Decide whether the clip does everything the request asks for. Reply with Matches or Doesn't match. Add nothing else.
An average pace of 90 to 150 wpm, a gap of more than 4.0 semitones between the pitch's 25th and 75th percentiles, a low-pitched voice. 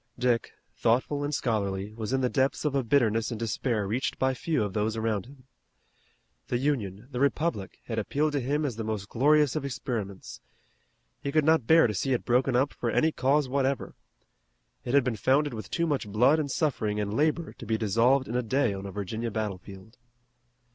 Doesn't match